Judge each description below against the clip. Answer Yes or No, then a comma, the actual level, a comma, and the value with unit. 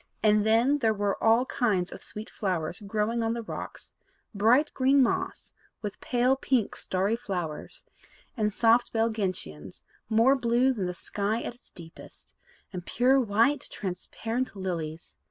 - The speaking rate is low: No, average, 150 wpm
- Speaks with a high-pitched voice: Yes, high, 220 Hz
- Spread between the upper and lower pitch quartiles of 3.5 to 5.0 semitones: Yes, average, 3.8 semitones